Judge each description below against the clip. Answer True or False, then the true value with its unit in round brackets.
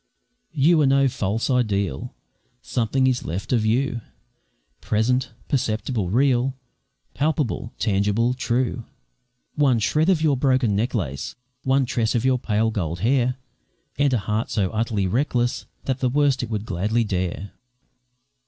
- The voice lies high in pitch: False (120 Hz)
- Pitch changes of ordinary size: True (3.8 semitones)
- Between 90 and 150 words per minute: True (135 wpm)